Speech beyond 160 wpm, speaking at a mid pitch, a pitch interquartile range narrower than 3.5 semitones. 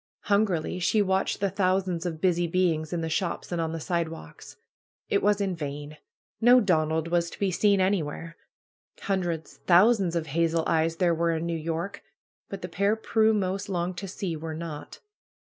Yes: average, 175 wpm; medium, 175 Hz; average, 3.0 semitones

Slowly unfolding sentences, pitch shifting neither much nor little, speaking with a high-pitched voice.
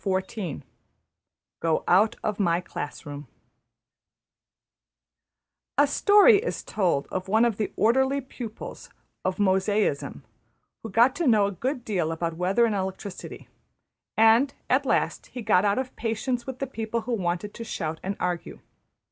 No: average, 145 wpm; average, 4.5 semitones; high, 210 Hz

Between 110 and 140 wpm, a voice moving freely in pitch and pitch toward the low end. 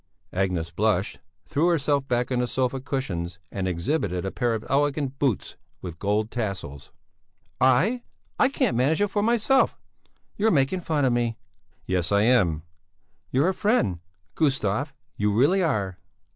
No: average, 155 wpm; wide, 7.2 semitones; low, 125 Hz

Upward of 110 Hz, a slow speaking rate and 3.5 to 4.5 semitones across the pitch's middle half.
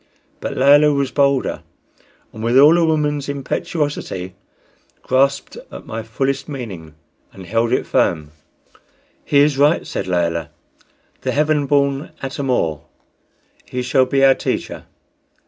Yes: low, 135 Hz; slow, 130 wpm; average, 4.2 semitones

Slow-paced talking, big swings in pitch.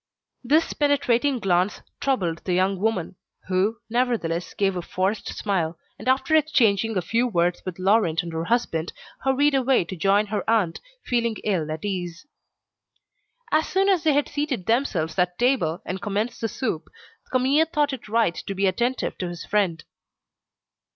No: average, 165 wpm; wide, 6.2 semitones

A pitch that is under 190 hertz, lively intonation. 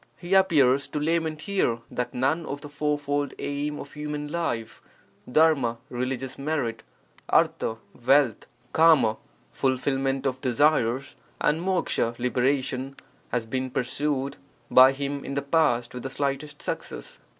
No: medium, 140 Hz; average, 2.8 semitones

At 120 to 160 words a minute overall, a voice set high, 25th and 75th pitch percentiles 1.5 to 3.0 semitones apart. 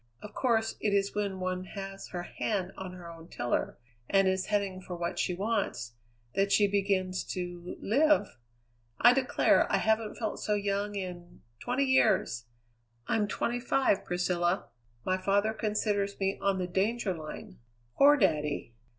Yes: average, 155 wpm; high, 195 Hz; average, 2.7 semitones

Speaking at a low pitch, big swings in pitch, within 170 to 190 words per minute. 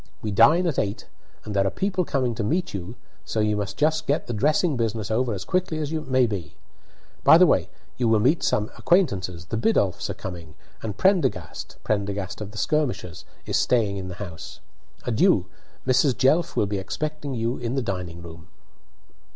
Yes: low, 110 Hz; wide, 6.7 semitones; average, 185 wpm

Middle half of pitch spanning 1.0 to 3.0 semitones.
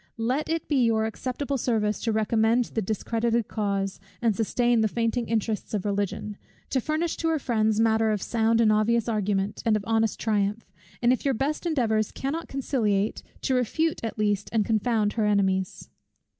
Yes: narrow, 2.5 semitones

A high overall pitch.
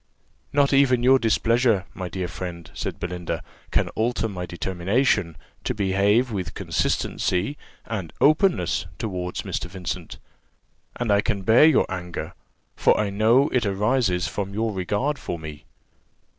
No: low, 100 Hz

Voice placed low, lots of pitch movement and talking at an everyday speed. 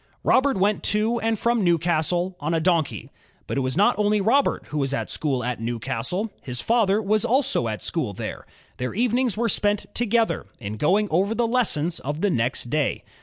No: high, 190 Hz; wide, 7.3 semitones; average, 190 wpm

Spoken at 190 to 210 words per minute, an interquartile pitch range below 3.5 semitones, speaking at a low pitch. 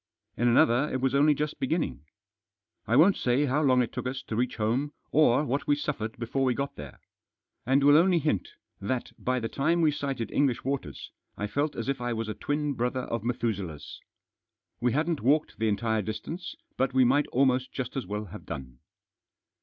No: average, 195 wpm; average, 3.8 semitones; low, 130 Hz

